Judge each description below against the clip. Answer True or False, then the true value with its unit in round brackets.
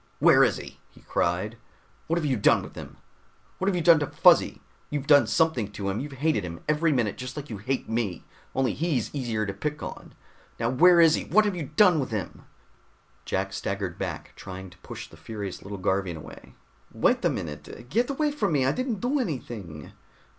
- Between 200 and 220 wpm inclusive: True (205 wpm)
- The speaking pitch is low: True (130 Hz)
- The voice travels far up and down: True (8.2 semitones)